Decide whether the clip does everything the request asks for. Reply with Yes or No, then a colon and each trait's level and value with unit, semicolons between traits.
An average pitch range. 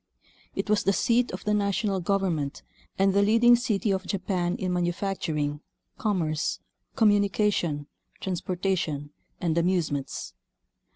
Yes: average, 3.3 semitones